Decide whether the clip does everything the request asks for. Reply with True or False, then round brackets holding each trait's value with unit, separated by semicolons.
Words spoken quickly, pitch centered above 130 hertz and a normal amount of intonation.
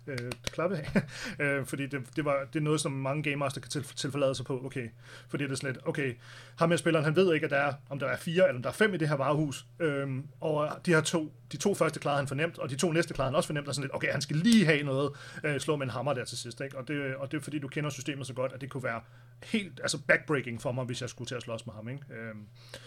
True (305 wpm; 140 Hz; 3.2 semitones)